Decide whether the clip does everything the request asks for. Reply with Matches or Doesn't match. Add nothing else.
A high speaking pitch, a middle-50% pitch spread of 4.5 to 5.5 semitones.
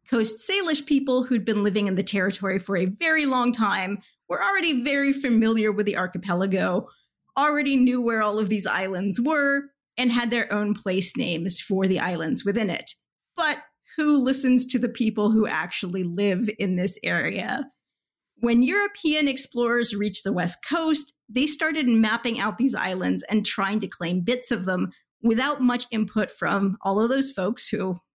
Matches